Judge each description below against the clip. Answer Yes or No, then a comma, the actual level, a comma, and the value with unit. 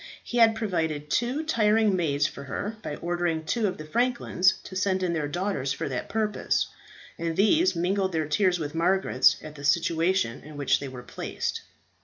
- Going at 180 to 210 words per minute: Yes, average, 185 wpm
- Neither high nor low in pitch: Yes, medium, 175 Hz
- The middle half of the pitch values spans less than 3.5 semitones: No, wide, 5.4 semitones